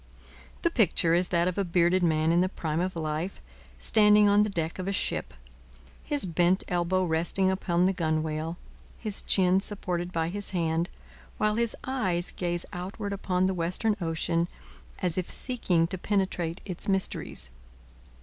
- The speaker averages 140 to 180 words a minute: Yes, average, 160 wpm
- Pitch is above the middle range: No, medium, 180 Hz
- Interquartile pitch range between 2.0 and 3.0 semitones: Yes, narrow, 2.6 semitones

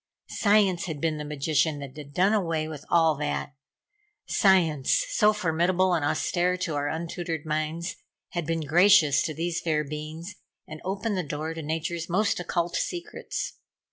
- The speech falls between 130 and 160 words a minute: Yes, average, 155 wpm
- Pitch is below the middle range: No, medium, 165 Hz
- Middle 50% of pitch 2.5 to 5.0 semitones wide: Yes, average, 3.0 semitones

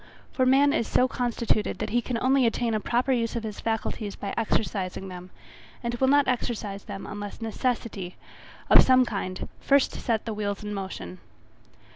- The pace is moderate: Yes, average, 175 wpm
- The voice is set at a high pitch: Yes, high, 225 Hz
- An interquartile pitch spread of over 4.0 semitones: No, average, 3.7 semitones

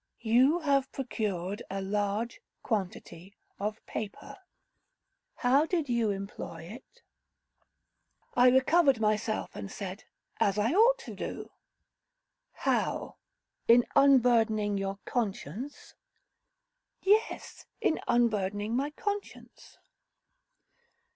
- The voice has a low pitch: No, high, 225 Hz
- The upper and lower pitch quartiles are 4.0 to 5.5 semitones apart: Yes, average, 5.1 semitones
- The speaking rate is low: Yes, slow, 95 wpm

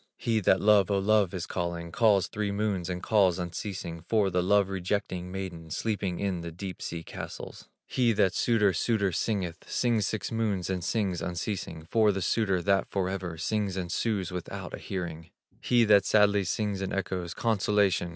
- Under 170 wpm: No, average, 175 wpm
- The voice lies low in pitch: Yes, very low, 95 Hz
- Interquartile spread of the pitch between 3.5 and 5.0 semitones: No, average, 2.8 semitones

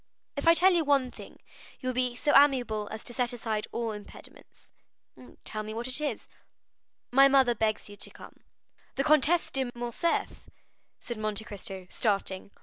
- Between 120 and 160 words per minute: No, average, 170 wpm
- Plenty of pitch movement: No, average, 4.1 semitones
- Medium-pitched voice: No, high, 245 Hz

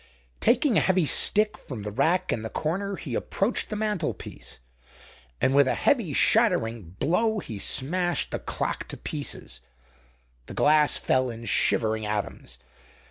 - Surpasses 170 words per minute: No, average, 145 wpm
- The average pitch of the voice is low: No, medium, 155 Hz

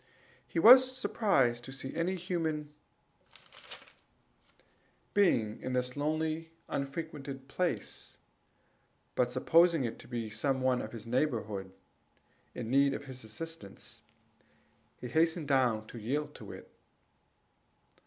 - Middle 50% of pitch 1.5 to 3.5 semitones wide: No, average, 5.0 semitones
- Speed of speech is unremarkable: No, slow, 115 wpm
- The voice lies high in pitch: No, low, 135 Hz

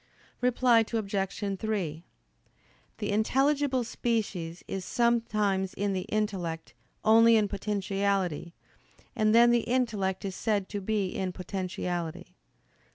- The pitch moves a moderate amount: Yes, average, 3.3 semitones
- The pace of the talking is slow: Yes, slow, 110 wpm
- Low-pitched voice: No, high, 205 Hz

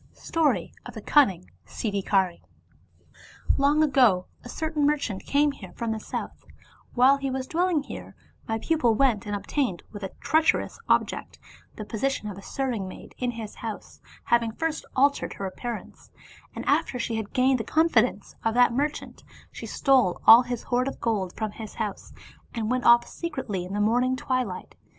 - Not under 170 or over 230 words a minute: Yes, average, 175 wpm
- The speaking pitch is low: No, high, 240 Hz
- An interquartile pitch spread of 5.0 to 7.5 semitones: No, average, 4.5 semitones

